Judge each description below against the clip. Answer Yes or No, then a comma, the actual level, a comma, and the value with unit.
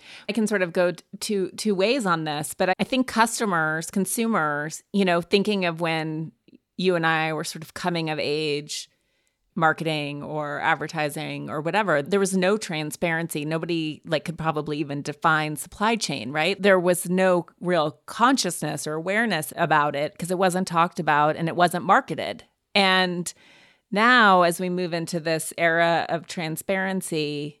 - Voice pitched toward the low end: No, medium, 170 Hz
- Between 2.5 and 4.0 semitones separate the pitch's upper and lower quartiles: Yes, average, 3.5 semitones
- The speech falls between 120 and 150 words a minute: No, average, 165 wpm